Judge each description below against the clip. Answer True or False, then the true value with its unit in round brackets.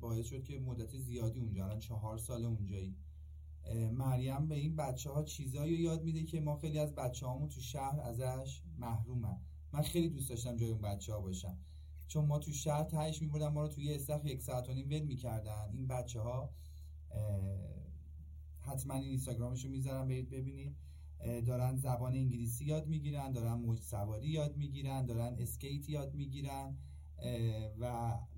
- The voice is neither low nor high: False (120 Hz)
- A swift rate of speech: True (165 wpm)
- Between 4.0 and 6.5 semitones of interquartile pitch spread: True (5.6 semitones)